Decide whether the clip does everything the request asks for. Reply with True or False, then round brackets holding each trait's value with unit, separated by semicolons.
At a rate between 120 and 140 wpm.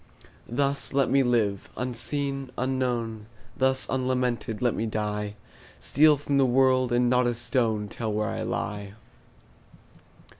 True (135 wpm)